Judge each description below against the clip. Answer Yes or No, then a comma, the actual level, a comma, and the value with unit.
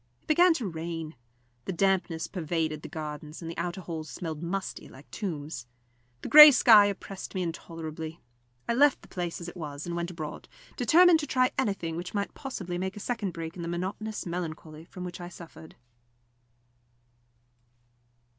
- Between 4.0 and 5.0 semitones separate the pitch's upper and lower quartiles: No, average, 3.6 semitones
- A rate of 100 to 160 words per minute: No, average, 170 wpm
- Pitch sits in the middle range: Yes, medium, 175 Hz